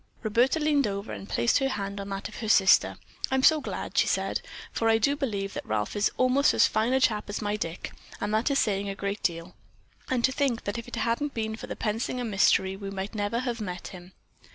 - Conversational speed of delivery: No, fast, 235 wpm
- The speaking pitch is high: Yes, high, 215 Hz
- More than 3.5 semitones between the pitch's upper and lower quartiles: Yes, average, 4.0 semitones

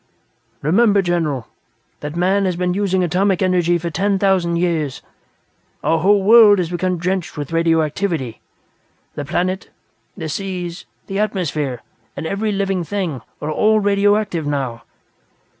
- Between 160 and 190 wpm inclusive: No, slow, 135 wpm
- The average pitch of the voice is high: No, medium, 180 Hz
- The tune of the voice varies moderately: Yes, average, 3.5 semitones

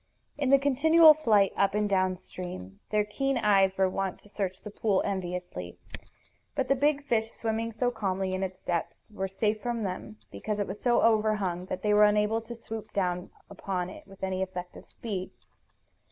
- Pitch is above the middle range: Yes, high, 205 Hz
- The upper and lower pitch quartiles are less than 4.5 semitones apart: Yes, average, 3.3 semitones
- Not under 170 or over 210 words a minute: Yes, average, 180 wpm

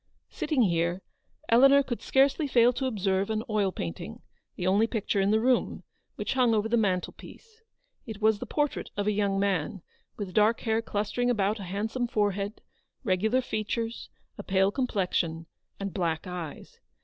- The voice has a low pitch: No, high, 210 Hz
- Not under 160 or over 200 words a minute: Yes, average, 175 wpm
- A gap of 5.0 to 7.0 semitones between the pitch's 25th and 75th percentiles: No, average, 3.6 semitones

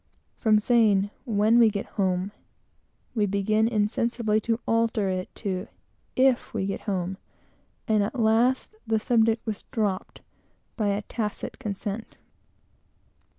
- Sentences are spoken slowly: Yes, slow, 125 wpm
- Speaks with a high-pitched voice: Yes, high, 215 Hz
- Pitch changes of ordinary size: No, narrow, 2.2 semitones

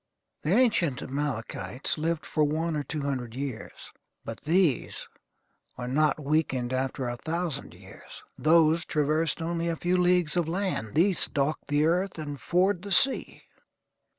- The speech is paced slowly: No, average, 150 wpm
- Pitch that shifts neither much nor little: Yes, average, 3.6 semitones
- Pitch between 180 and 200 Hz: No, medium, 155 Hz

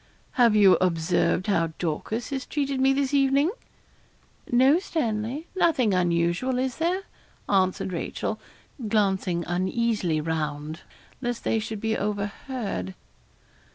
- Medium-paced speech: No, slow, 115 wpm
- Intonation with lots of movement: Yes, wide, 6.9 semitones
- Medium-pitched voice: No, high, 215 Hz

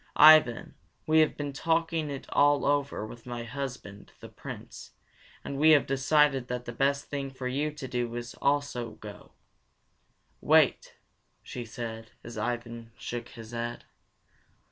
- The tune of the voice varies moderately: Yes, average, 3.4 semitones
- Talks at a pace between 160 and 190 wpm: No, average, 150 wpm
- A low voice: Yes, low, 130 Hz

